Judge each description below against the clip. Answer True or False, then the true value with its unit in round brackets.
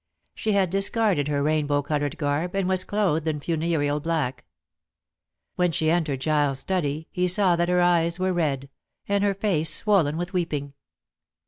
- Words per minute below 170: True (160 wpm)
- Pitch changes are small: False (4.0 semitones)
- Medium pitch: True (165 Hz)